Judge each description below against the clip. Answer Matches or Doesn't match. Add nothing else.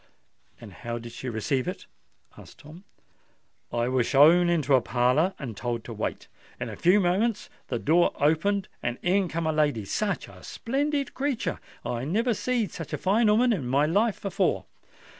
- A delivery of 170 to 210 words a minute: Matches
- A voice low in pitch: Doesn't match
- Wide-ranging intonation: Matches